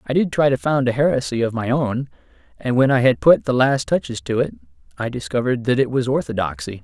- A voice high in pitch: No, low, 125 Hz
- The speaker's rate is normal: No, fast, 230 wpm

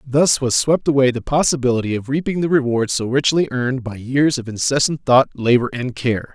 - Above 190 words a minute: Yes, average, 200 wpm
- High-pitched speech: No, low, 130 Hz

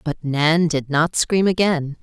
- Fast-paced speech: No, average, 180 wpm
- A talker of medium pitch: Yes, medium, 160 Hz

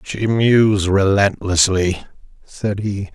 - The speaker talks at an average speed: No, slow, 95 wpm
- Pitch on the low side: Yes, low, 100 Hz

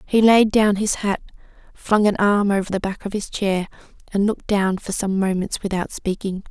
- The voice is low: No, high, 200 Hz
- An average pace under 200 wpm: No, fast, 205 wpm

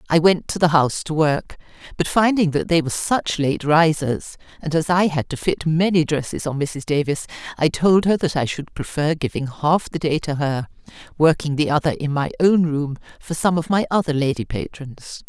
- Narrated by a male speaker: No, female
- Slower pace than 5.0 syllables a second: No, 5.1 syllables/s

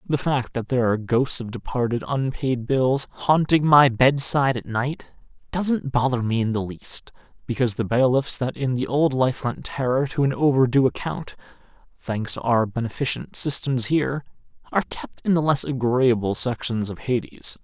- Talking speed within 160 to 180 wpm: Yes, average, 170 wpm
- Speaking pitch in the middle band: No, low, 125 Hz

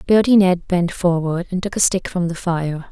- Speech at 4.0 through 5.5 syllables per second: Yes, 4.8 syllables/s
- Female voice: Yes, female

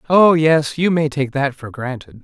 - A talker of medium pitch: Yes, medium, 145 Hz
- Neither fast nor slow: No, fast, 215 wpm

